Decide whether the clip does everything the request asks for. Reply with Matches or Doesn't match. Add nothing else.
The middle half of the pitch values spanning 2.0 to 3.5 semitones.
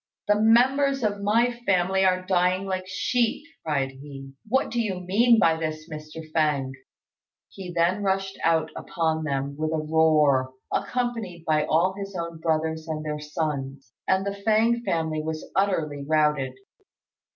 Doesn't match